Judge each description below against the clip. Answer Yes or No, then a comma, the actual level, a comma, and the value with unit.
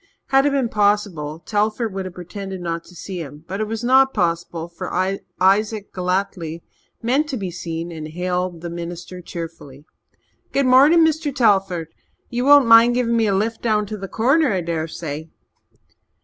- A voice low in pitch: No, high, 195 Hz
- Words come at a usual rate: Yes, average, 170 wpm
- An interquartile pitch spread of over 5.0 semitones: Yes, wide, 5.4 semitones